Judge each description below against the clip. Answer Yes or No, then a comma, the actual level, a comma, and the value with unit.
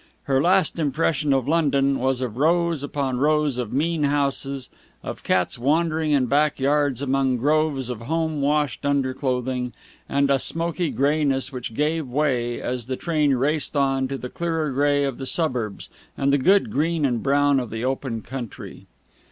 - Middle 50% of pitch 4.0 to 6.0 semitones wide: No, average, 2.7 semitones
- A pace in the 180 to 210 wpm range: No, average, 170 wpm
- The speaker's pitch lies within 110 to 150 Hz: Yes, medium, 140 Hz